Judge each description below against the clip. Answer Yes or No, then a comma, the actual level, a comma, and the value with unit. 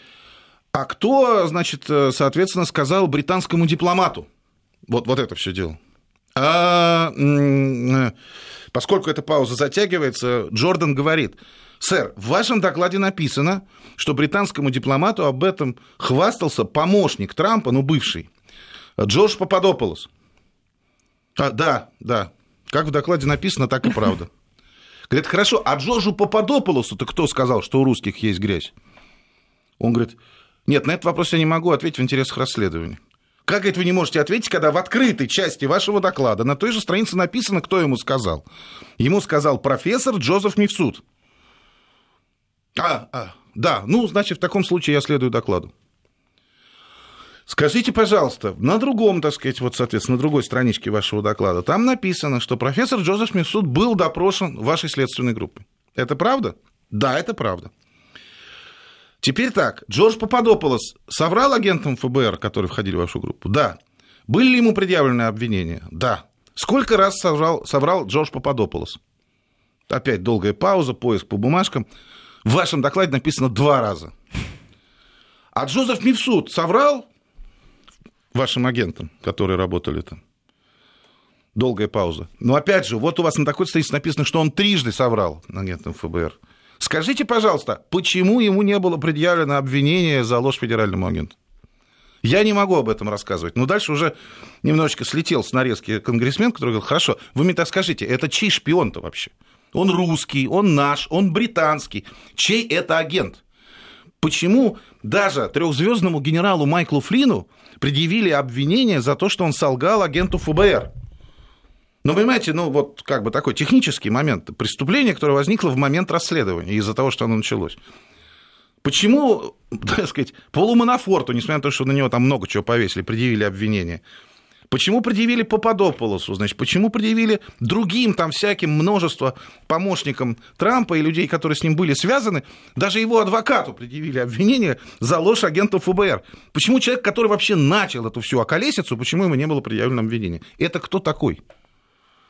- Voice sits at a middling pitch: Yes, medium, 155 Hz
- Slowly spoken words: No, average, 145 wpm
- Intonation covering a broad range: Yes, wide, 7.5 semitones